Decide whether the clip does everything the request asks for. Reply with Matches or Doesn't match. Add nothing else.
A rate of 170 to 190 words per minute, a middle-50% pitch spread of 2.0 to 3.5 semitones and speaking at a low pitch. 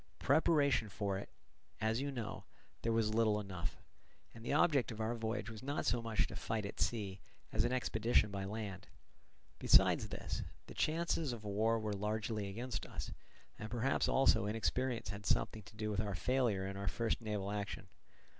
Matches